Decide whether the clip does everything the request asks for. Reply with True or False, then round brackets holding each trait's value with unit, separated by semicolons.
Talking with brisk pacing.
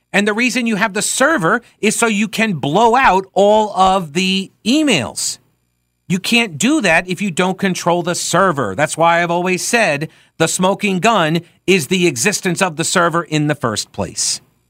False (185 wpm)